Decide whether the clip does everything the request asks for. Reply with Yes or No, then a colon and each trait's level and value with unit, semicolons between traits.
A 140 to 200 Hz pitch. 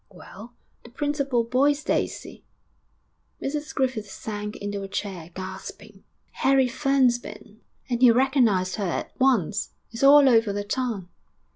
No: high, 240 Hz